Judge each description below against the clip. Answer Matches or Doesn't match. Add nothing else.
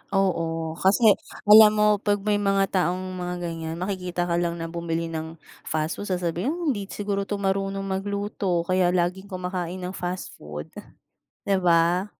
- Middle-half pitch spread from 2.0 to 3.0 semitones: Matches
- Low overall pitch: Doesn't match